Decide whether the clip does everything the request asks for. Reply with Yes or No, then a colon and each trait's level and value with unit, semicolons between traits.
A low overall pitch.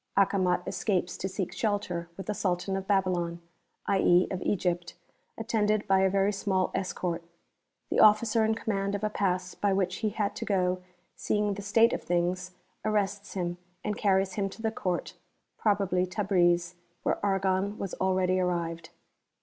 No: high, 190 Hz